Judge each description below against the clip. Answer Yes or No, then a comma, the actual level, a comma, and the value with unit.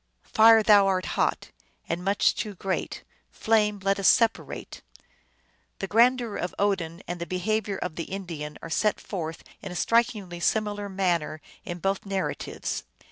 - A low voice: No, high, 195 Hz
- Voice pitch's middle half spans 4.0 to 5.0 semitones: No, average, 3.2 semitones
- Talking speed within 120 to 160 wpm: Yes, average, 155 wpm